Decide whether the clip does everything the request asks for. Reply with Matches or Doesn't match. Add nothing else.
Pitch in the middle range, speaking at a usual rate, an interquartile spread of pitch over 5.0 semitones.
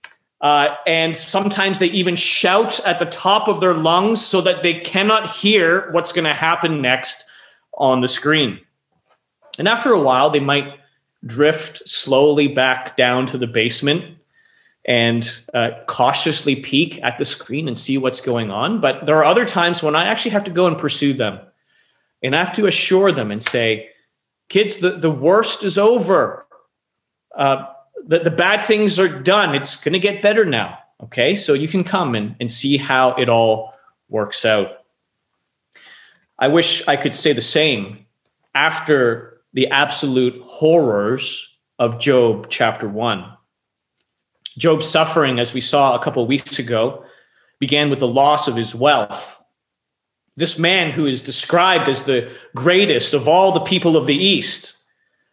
Matches